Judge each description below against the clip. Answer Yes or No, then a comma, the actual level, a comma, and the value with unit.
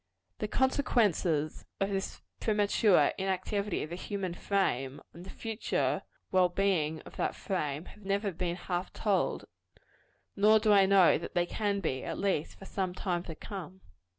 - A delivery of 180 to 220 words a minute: No, average, 160 wpm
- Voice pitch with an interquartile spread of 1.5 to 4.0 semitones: Yes, narrow, 2.6 semitones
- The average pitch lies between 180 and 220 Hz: Yes, high, 190 Hz